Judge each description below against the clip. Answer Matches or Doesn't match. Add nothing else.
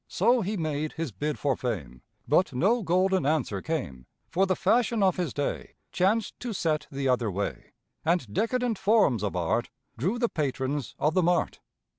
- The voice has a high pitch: Doesn't match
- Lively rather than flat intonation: Matches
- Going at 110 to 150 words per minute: Doesn't match